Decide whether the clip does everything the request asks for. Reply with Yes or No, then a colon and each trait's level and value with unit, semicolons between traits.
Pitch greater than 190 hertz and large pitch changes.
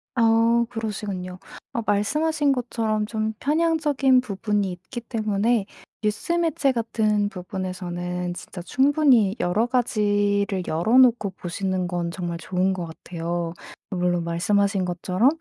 No: high, 205 Hz; average, 4.6 semitones